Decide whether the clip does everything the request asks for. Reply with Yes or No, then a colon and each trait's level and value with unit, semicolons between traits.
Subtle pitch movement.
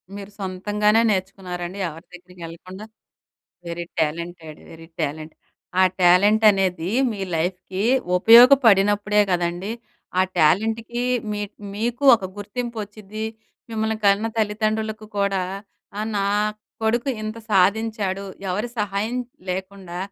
No: average, 3.1 semitones